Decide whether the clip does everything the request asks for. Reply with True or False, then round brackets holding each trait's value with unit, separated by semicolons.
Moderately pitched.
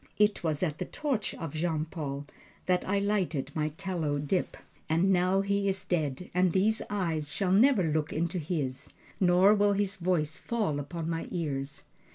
True (175 Hz)